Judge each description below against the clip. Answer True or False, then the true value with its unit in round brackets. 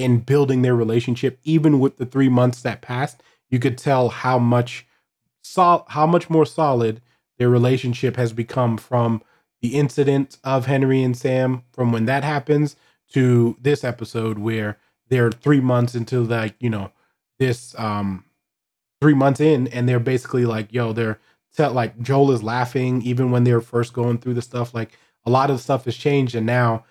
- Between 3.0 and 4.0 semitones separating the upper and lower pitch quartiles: False (2.4 semitones)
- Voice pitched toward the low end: True (125 Hz)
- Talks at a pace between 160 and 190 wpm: True (180 wpm)